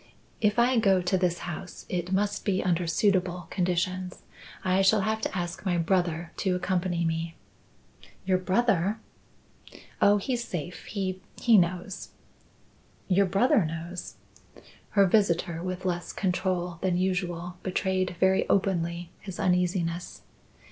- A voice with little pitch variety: Yes, narrow, 1.8 semitones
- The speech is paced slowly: Yes, slow, 130 wpm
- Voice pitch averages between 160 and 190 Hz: Yes, medium, 185 Hz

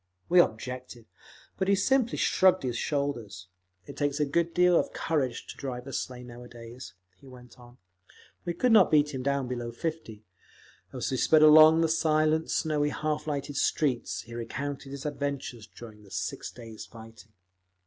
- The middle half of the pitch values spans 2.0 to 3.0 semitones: No, average, 4.4 semitones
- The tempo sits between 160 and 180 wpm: Yes, average, 170 wpm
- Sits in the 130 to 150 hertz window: Yes, medium, 140 Hz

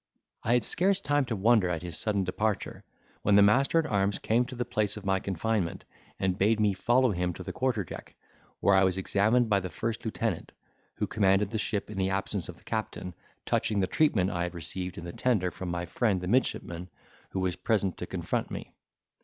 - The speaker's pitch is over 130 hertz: No, low, 100 Hz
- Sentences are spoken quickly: Yes, fast, 215 wpm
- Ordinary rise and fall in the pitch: Yes, average, 3.5 semitones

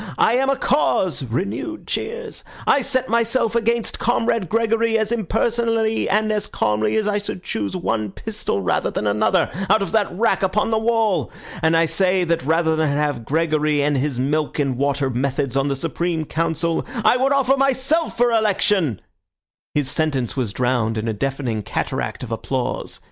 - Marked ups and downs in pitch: Yes, wide, 8.5 semitones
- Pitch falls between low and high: Yes, medium, 175 Hz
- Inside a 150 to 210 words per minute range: Yes, average, 175 wpm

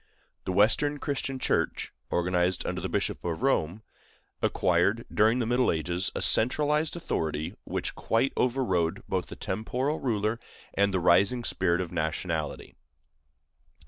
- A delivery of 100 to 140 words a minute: Yes, slow, 135 wpm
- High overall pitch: No, low, 100 Hz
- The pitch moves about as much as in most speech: No, wide, 6.2 semitones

